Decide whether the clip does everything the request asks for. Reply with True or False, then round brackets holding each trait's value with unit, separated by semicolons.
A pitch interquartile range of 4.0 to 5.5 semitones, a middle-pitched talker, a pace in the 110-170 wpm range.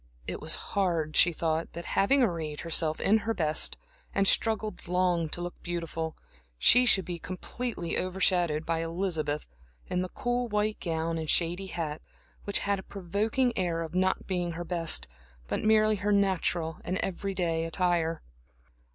False (3.2 semitones; 175 Hz; 160 wpm)